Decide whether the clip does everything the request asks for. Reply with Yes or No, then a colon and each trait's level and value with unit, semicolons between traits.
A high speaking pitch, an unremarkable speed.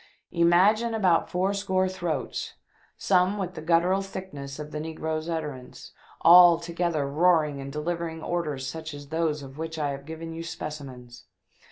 No: medium, 165 Hz; average, 165 wpm